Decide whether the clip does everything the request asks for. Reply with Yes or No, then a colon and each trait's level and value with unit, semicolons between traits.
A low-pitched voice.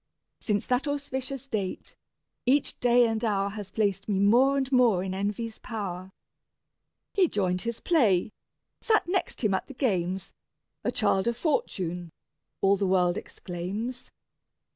No: high, 215 Hz